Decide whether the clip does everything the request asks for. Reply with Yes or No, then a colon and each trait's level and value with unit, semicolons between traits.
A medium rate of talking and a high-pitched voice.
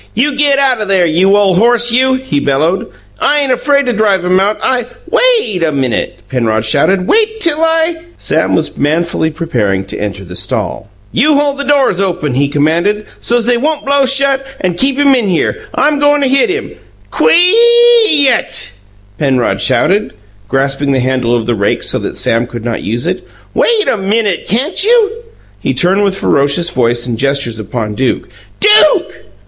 Yes: average, 185 wpm; high, 200 Hz